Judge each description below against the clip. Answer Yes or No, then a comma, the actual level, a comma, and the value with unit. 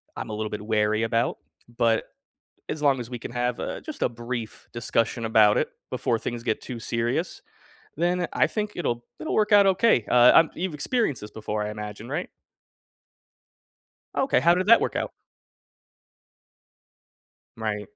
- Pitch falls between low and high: No, low, 120 Hz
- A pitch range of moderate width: No, wide, 7.5 semitones